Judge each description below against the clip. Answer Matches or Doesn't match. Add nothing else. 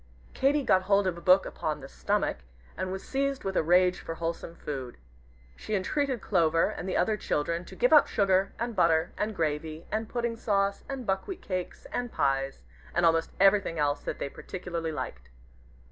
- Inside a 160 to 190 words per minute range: Matches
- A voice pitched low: Doesn't match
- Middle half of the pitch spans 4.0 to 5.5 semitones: Matches